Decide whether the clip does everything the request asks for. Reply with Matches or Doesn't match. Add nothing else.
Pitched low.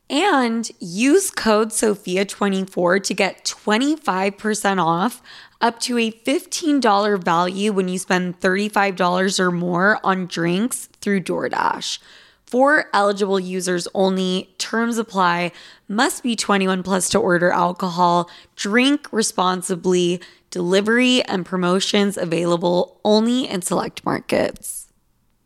Doesn't match